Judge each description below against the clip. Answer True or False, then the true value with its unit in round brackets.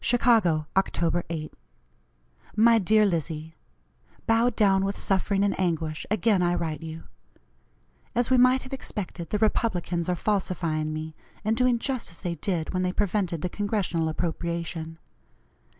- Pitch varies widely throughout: False (4.5 semitones)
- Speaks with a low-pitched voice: False (185 Hz)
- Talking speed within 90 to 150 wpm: True (145 wpm)